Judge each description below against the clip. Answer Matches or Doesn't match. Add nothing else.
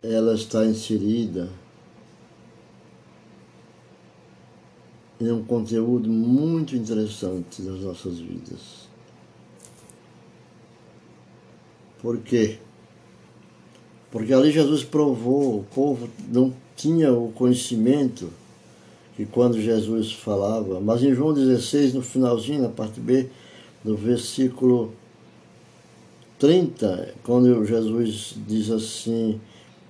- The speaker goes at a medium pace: Doesn't match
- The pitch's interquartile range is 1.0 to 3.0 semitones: Matches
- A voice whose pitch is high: Doesn't match